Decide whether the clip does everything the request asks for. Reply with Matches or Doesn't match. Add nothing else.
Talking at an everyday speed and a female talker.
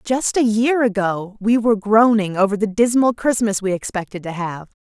Matches